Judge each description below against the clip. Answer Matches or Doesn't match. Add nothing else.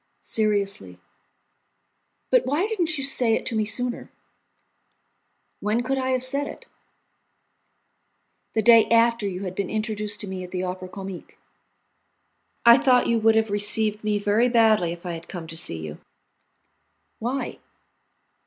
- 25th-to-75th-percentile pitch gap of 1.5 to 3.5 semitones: Doesn't match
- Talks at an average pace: Matches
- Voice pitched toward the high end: Matches